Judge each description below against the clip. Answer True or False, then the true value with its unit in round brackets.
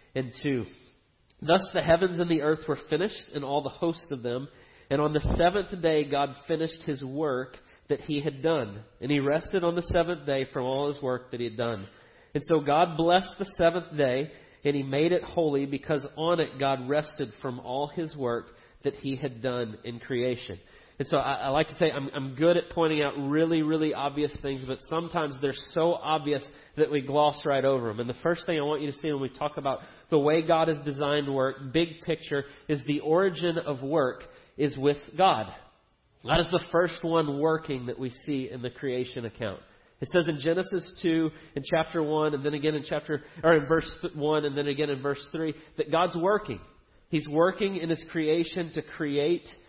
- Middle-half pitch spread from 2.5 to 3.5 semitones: True (3.1 semitones)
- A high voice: False (150 Hz)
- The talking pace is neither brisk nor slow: False (210 wpm)